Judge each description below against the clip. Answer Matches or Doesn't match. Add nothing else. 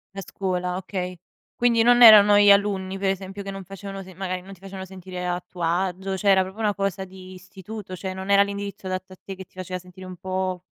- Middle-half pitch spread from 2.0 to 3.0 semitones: Doesn't match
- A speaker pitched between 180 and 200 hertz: Matches